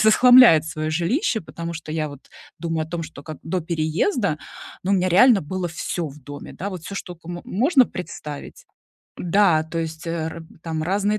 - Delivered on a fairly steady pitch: No, average, 3.6 semitones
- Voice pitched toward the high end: No, medium, 170 Hz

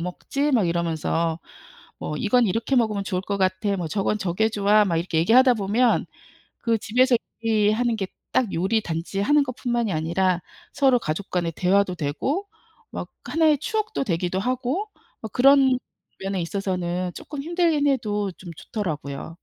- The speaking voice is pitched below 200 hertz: No, high, 205 Hz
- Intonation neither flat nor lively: No, wide, 6.0 semitones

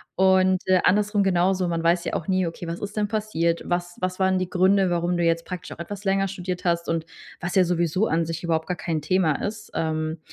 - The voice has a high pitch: No, medium, 180 Hz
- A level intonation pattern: Yes, narrow, 2.1 semitones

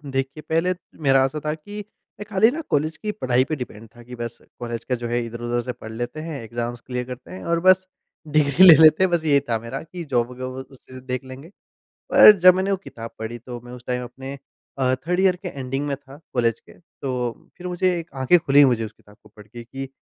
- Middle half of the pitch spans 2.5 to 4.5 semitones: No, average, 5.1 semitones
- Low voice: Yes, low, 130 Hz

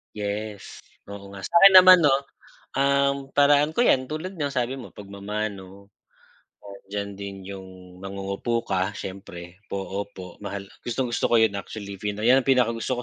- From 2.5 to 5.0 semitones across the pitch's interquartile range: No, wide, 5.5 semitones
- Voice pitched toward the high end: No, low, 105 Hz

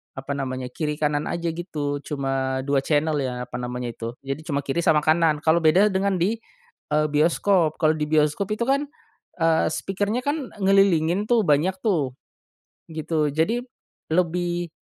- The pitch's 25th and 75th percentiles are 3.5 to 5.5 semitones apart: Yes, average, 4.0 semitones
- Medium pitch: Yes, medium, 155 Hz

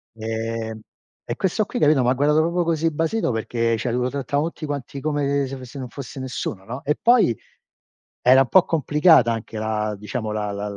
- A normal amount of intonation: Yes, average, 4.8 semitones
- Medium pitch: No, low, 130 Hz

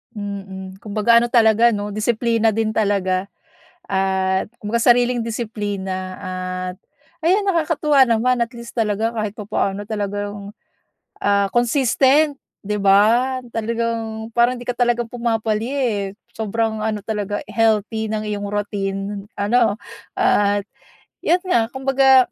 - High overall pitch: Yes, high, 220 Hz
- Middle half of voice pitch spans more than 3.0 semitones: No, average, 2.7 semitones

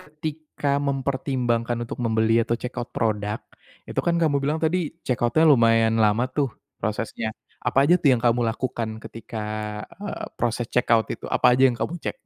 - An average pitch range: Yes, average, 3.7 semitones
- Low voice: Yes, low, 120 Hz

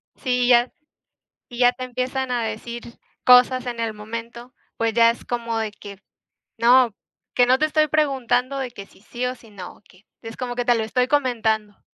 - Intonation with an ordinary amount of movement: No, narrow, 2.0 semitones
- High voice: Yes, high, 240 Hz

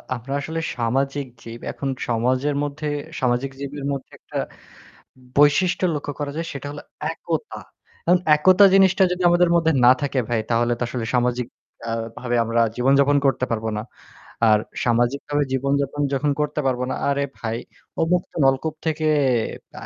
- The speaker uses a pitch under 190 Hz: Yes, medium, 140 Hz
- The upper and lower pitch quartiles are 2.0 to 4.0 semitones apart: Yes, average, 3.2 semitones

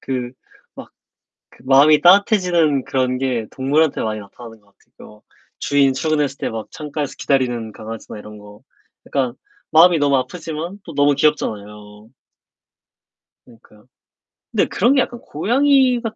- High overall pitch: No, low, 135 Hz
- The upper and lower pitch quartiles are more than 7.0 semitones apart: No, wide, 6.1 semitones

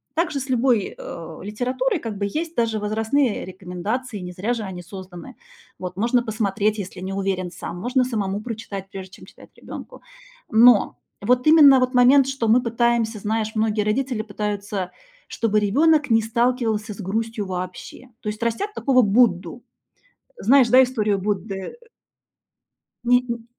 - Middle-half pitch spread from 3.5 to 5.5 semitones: Yes, average, 3.8 semitones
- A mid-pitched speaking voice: No, high, 220 Hz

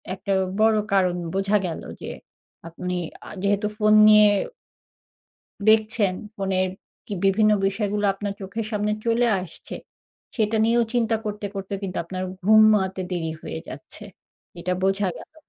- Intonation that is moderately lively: No, narrow, 2.2 semitones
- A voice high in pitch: Yes, high, 205 Hz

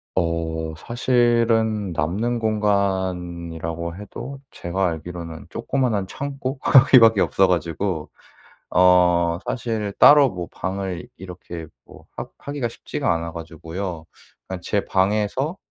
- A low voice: Yes, very low, 95 Hz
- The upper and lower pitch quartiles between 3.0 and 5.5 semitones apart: Yes, average, 5.1 semitones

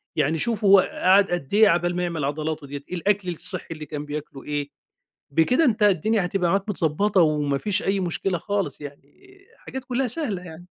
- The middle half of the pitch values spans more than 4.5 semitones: Yes, average, 5.0 semitones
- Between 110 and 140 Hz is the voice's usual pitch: No, medium, 175 Hz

